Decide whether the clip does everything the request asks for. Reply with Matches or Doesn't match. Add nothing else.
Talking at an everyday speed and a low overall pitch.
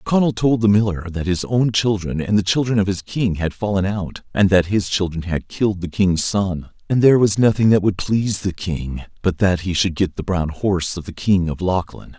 Doesn't match